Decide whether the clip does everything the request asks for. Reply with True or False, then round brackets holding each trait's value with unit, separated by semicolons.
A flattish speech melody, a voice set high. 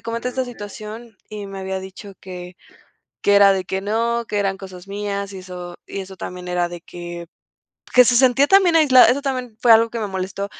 False (3.8 semitones; 200 Hz)